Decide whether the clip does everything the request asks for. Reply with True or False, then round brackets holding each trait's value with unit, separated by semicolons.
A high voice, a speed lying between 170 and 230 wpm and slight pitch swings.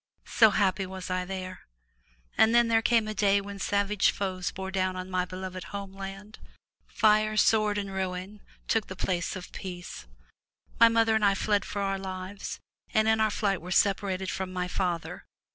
True (195 Hz; 180 wpm; 2.2 semitones)